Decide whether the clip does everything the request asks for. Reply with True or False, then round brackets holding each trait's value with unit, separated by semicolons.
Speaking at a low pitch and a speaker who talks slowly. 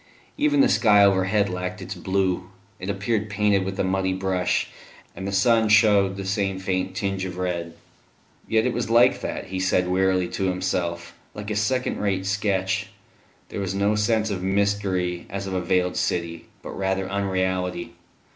False (95 Hz; 175 wpm)